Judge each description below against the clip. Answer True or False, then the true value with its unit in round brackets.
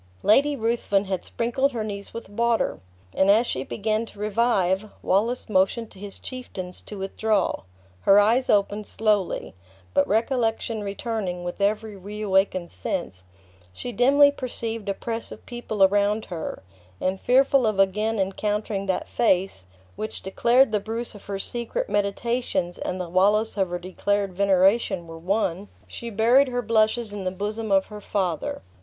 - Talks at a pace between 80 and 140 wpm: False (155 wpm)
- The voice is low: False (210 Hz)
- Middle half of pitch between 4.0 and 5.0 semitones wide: False (3.1 semitones)